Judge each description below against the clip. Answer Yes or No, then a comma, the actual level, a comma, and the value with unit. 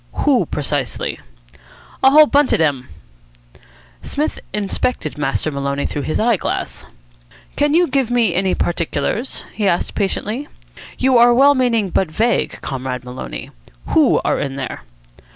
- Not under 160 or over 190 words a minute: No, average, 140 wpm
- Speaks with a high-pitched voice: Yes, high, 205 Hz